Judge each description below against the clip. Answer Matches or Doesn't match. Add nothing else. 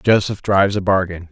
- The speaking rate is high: Doesn't match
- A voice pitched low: Matches